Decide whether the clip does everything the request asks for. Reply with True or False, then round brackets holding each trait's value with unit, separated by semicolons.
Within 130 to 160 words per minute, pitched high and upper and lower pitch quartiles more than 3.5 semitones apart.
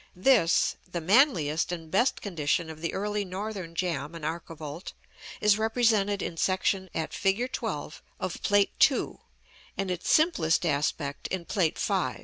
False (145 wpm; 180 Hz; 4.1 semitones)